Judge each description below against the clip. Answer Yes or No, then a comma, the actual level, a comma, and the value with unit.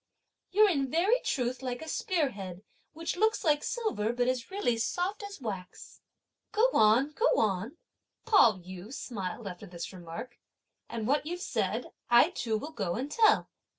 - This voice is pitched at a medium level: No, very high, 255 Hz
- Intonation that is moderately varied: No, wide, 8.9 semitones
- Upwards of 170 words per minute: No, average, 165 wpm